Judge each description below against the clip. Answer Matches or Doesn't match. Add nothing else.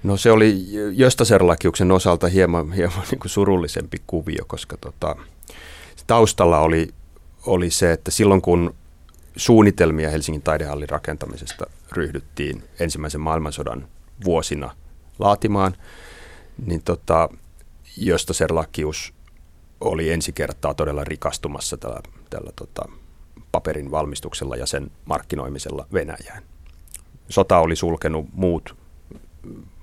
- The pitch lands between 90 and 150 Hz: Doesn't match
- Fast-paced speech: Doesn't match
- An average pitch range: Matches